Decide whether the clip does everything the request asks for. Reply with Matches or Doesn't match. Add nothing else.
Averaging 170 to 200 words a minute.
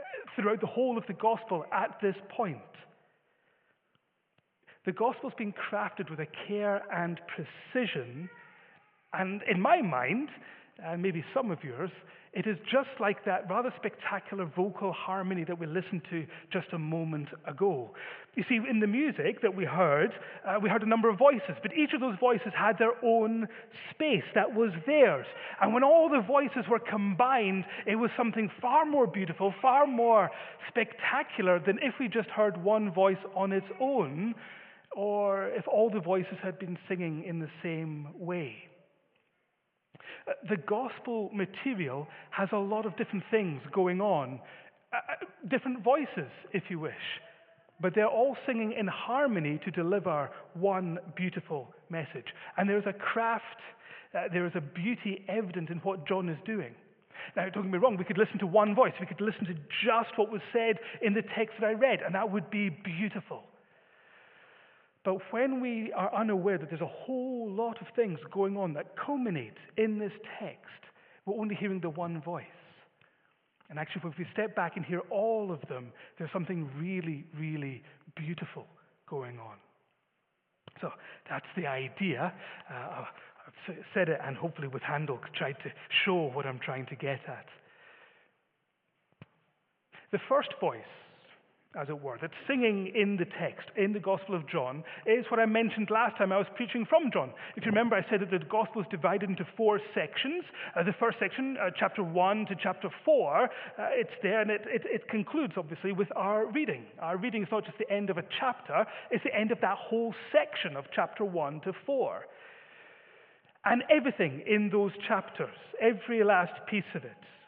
Matches